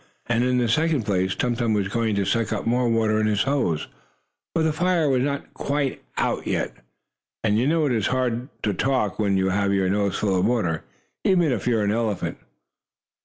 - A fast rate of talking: Yes, fast, 215 wpm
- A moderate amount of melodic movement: Yes, average, 4.4 semitones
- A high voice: No, low, 115 Hz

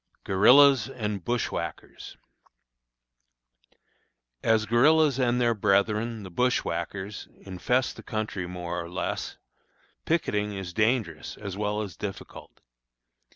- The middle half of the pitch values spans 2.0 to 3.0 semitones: No, average, 3.8 semitones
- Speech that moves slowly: Yes, slow, 105 wpm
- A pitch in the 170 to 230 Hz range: No, low, 105 Hz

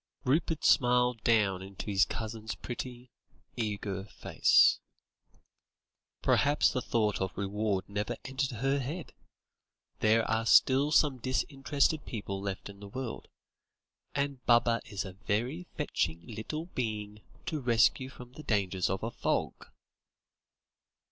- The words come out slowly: Yes, slow, 125 wpm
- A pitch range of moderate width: Yes, average, 4.4 semitones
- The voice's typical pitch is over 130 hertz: No, low, 115 Hz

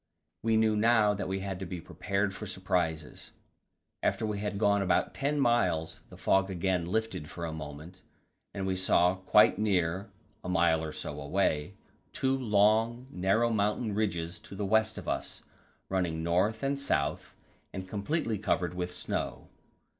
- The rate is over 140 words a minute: Yes, average, 160 wpm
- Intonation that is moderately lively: Yes, average, 3.5 semitones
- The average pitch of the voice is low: Yes, very low, 95 Hz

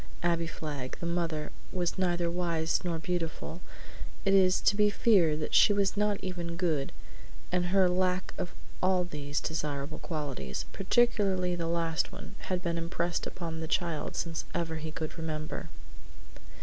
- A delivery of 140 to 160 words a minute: Yes, average, 155 wpm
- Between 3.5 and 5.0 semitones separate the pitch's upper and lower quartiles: No, narrow, 2.5 semitones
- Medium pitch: Yes, medium, 170 Hz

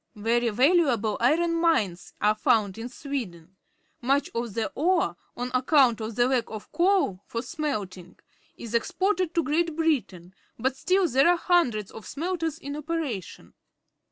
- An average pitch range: No, wide, 7.1 semitones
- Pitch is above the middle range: Yes, very high, 255 Hz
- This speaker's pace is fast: No, average, 145 wpm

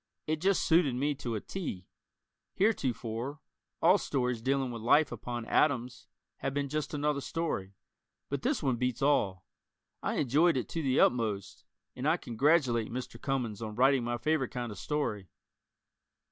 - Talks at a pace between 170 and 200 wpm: No, average, 160 wpm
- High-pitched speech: No, low, 130 Hz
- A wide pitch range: No, average, 4.0 semitones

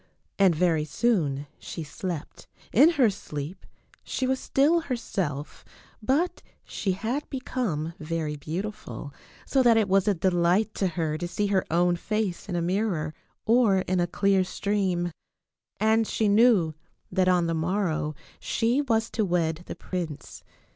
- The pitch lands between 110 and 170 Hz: No, medium, 185 Hz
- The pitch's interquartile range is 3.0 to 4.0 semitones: No, average, 4.8 semitones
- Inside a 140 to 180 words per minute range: Yes, average, 150 wpm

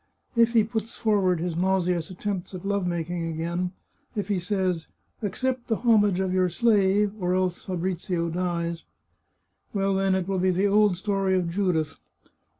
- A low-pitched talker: No, medium, 185 Hz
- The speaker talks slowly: No, average, 170 wpm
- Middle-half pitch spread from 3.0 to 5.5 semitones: No, narrow, 2.5 semitones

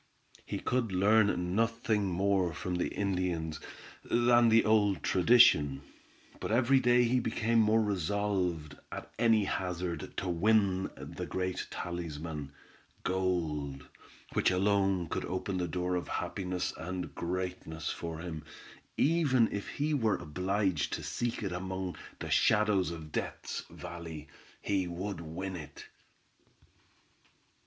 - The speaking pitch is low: Yes, very low, 95 Hz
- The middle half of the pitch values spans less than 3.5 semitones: No, average, 3.8 semitones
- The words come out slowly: Yes, slow, 125 wpm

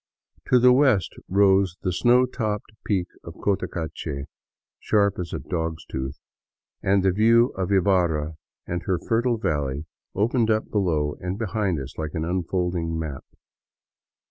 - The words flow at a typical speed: Yes, average, 145 wpm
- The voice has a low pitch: Yes, very low, 95 Hz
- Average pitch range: Yes, average, 4.7 semitones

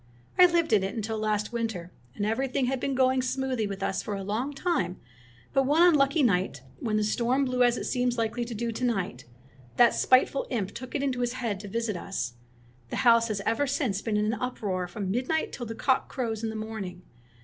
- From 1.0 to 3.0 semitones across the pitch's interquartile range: No, average, 3.6 semitones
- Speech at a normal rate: No, fast, 220 wpm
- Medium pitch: No, high, 230 Hz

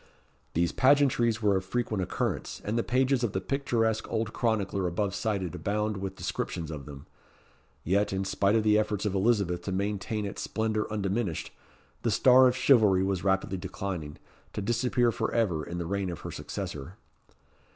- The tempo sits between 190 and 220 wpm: No, average, 170 wpm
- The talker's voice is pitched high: No, low, 100 Hz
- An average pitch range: Yes, average, 3.2 semitones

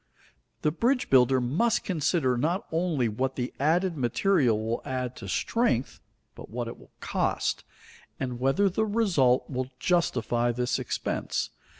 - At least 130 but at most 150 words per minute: Yes, average, 140 wpm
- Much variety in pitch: Yes, wide, 6.3 semitones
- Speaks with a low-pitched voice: Yes, low, 130 Hz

